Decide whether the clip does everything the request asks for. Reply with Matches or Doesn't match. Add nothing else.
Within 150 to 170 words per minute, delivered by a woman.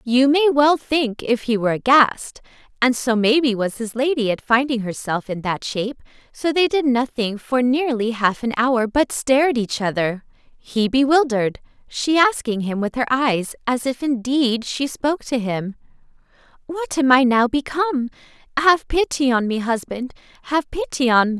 Doesn't match